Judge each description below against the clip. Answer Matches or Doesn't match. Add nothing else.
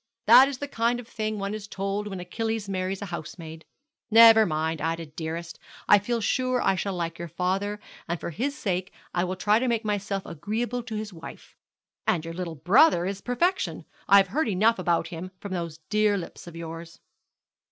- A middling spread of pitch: Matches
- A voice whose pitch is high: Matches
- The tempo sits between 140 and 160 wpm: Doesn't match